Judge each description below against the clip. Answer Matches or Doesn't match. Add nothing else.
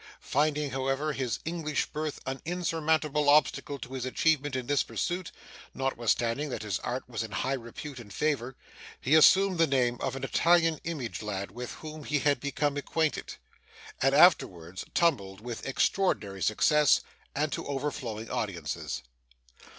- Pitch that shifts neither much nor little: Matches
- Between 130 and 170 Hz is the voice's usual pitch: Matches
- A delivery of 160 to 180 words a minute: Doesn't match